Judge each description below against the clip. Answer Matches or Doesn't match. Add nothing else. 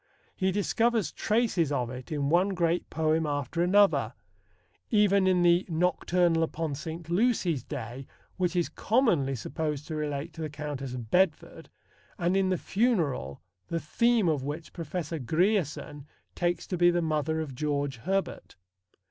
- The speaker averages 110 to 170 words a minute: Matches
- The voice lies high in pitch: Doesn't match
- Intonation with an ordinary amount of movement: Matches